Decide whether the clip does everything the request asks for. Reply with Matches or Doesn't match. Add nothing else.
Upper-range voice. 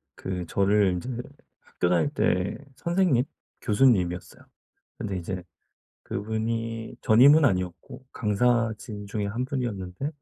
Doesn't match